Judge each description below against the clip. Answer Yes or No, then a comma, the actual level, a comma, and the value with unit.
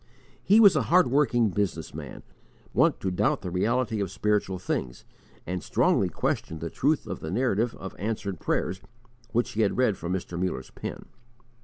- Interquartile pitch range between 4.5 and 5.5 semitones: Yes, average, 4.8 semitones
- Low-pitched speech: Yes, low, 100 Hz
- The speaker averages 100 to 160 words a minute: No, average, 175 wpm